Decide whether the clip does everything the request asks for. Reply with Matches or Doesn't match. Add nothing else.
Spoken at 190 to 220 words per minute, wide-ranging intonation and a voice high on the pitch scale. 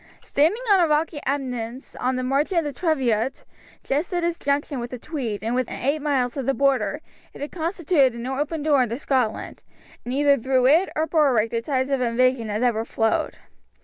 Doesn't match